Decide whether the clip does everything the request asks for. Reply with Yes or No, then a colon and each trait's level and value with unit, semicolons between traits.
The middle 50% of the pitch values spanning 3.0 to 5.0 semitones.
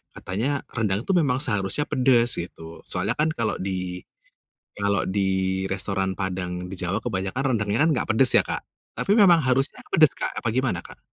No: wide, 5.5 semitones